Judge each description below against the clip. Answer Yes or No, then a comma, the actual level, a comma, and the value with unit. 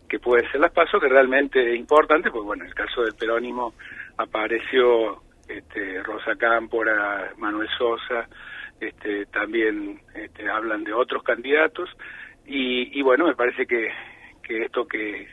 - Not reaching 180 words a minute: Yes, average, 150 wpm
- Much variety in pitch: No, average, 3.3 semitones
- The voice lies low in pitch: Yes, low, 125 Hz